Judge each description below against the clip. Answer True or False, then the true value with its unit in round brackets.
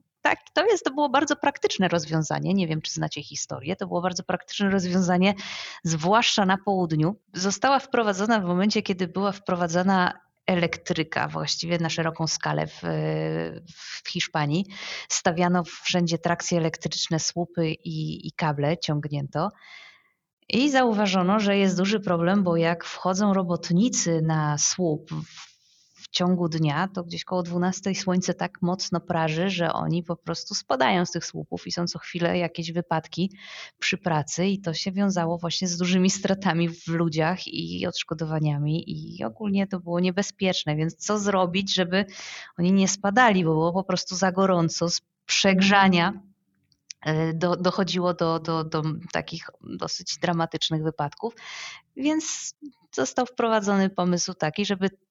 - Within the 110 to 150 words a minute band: True (140 wpm)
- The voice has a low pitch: False (180 Hz)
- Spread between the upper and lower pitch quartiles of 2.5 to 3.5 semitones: True (3.0 semitones)